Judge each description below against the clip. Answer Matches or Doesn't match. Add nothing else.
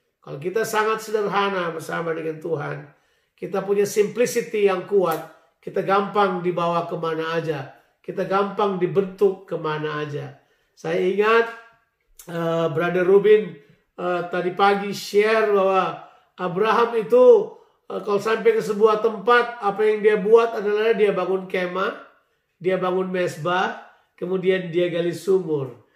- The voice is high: Matches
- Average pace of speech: Matches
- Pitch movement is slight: Doesn't match